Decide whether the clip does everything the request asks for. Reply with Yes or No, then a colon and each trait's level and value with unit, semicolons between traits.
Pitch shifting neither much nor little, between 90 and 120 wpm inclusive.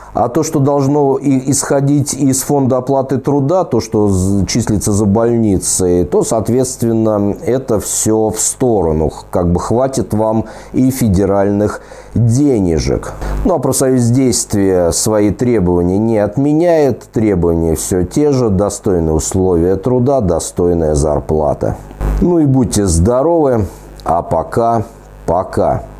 No: wide, 5.8 semitones; average, 115 wpm